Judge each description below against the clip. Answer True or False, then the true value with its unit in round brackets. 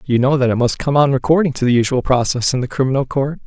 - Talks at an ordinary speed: False (275 wpm)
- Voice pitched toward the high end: False (135 Hz)